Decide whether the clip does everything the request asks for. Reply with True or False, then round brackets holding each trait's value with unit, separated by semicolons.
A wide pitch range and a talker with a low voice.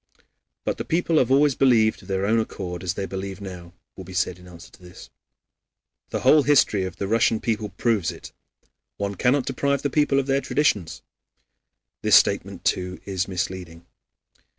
True (6.1 semitones; 100 Hz)